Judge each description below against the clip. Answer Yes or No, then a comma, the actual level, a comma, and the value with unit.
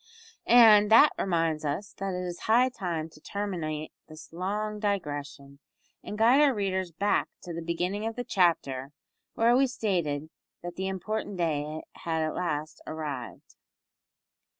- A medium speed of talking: Yes, average, 150 wpm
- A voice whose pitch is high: No, medium, 180 Hz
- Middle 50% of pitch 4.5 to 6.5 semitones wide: Yes, average, 5.0 semitones